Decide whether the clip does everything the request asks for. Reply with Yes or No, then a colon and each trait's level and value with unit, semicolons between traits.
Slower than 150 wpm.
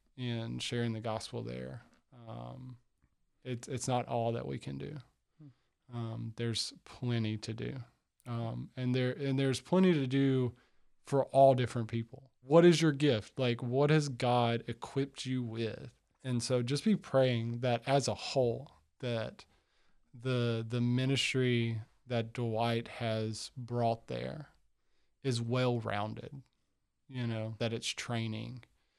Yes: average, 140 wpm